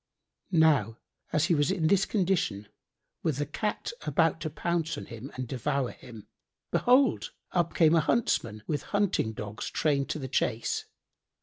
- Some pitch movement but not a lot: No, wide, 5.9 semitones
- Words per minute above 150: Yes, average, 160 wpm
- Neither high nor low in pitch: Yes, medium, 150 Hz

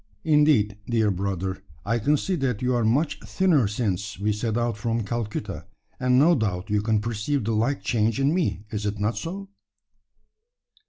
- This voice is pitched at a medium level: No, low, 115 Hz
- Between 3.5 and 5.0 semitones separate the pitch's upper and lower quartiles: Yes, average, 4.6 semitones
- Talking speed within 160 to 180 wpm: Yes, average, 175 wpm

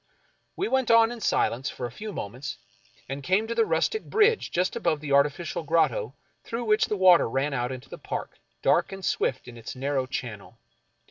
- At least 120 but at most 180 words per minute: No, average, 195 wpm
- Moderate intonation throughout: No, wide, 8.4 semitones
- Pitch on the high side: No, medium, 155 Hz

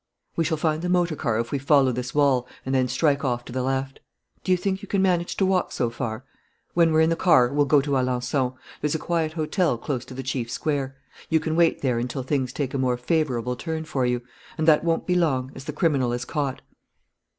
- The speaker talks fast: Yes, fast, 240 wpm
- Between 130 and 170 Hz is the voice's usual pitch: Yes, medium, 140 Hz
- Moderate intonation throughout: Yes, average, 4.0 semitones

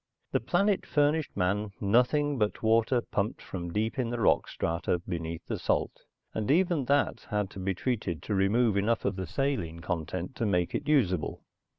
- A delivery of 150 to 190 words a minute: Yes, average, 180 wpm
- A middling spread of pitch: No, wide, 5.8 semitones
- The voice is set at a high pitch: No, low, 105 Hz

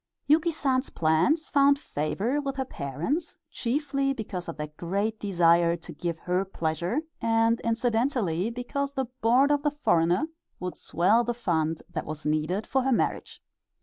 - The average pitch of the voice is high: Yes, high, 225 Hz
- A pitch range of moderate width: No, wide, 8.2 semitones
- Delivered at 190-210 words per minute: No, average, 155 wpm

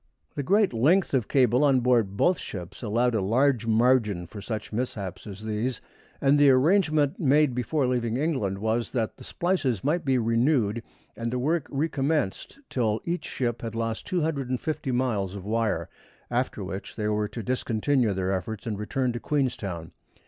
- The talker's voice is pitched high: No, low, 120 Hz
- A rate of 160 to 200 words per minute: Yes, average, 170 wpm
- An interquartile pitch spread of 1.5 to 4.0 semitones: No, average, 4.4 semitones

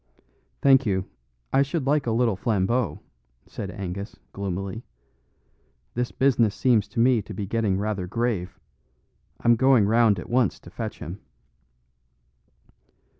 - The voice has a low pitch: Yes, low, 110 Hz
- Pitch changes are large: No, average, 4.0 semitones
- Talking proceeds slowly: Yes, slow, 130 wpm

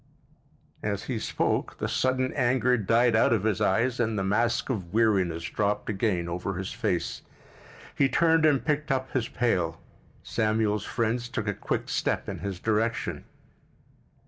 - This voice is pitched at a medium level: No, low, 110 Hz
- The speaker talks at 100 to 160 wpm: Yes, average, 155 wpm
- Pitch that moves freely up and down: No, average, 3.7 semitones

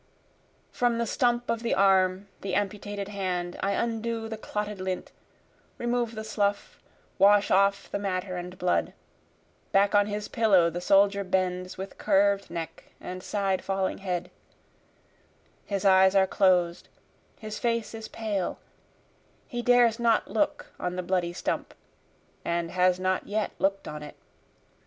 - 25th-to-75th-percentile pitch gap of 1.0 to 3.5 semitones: Yes, average, 2.7 semitones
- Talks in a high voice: Yes, high, 195 Hz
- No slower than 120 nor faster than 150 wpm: Yes, average, 145 wpm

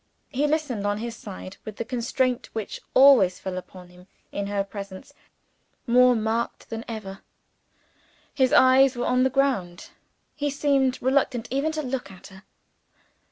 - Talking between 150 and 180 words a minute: Yes, average, 155 wpm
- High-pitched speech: Yes, high, 235 Hz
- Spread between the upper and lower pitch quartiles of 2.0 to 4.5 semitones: No, average, 5.0 semitones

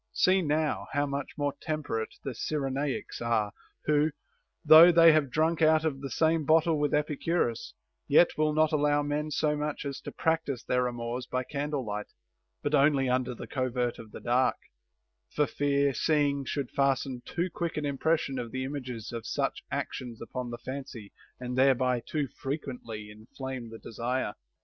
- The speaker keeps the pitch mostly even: No, average, 3.3 semitones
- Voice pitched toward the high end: No, medium, 140 Hz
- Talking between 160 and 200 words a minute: Yes, average, 170 wpm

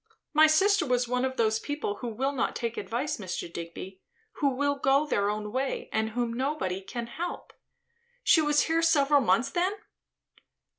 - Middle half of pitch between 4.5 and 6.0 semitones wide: Yes, average, 5.1 semitones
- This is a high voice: Yes, very high, 260 Hz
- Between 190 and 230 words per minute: No, average, 170 wpm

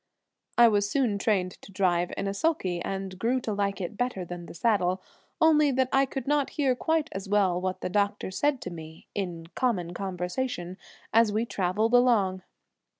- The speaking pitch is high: Yes, high, 200 Hz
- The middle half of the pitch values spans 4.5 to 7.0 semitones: Yes, average, 5.2 semitones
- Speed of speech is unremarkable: Yes, average, 185 wpm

